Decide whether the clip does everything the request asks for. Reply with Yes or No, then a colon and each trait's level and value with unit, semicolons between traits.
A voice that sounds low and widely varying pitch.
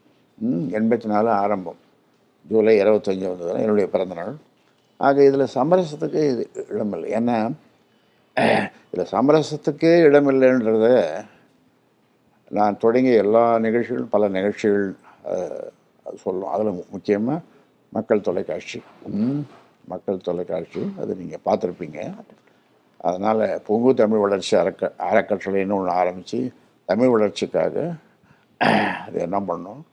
Yes: low, 110 Hz; wide, 5.8 semitones